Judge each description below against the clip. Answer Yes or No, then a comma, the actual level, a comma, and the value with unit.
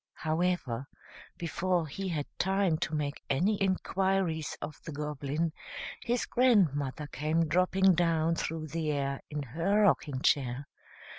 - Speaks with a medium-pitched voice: Yes, medium, 160 Hz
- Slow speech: Yes, slow, 130 wpm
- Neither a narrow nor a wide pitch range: Yes, average, 4.0 semitones